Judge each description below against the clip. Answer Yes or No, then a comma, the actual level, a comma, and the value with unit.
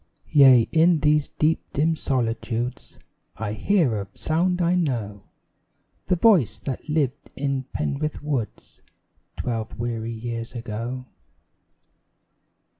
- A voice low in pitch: Yes, low, 130 Hz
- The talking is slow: Yes, slow, 110 wpm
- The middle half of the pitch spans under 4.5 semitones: No, average, 5.3 semitones